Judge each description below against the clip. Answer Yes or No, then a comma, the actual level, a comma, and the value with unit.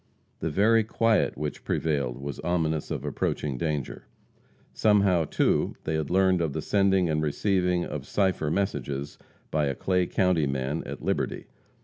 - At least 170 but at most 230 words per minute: No, average, 150 wpm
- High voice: No, very low, 80 Hz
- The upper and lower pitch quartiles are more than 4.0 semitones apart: Yes, average, 4.5 semitones